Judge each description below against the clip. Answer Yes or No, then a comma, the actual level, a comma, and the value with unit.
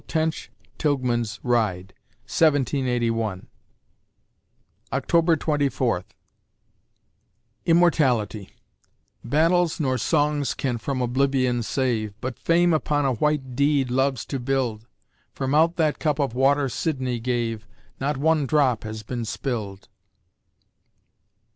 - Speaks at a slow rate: Yes, slow, 105 wpm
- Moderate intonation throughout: Yes, average, 3.9 semitones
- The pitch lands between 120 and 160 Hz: Yes, low, 135 Hz